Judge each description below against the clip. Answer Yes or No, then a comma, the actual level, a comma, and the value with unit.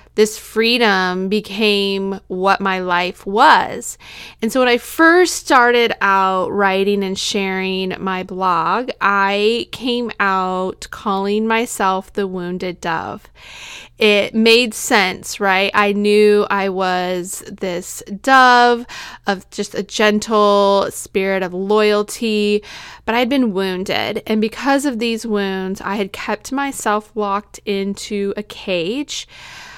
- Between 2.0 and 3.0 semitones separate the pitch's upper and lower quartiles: Yes, average, 2.7 semitones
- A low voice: No, high, 205 Hz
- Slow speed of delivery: Yes, slow, 125 wpm